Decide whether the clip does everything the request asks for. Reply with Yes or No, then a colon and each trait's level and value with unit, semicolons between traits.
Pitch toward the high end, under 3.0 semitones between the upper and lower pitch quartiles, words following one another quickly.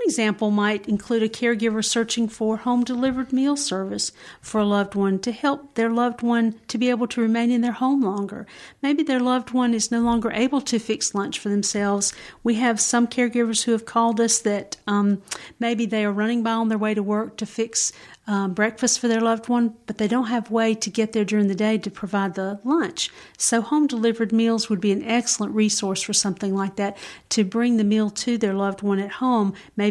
Yes: high, 225 Hz; narrow, 2.4 semitones; fast, 215 wpm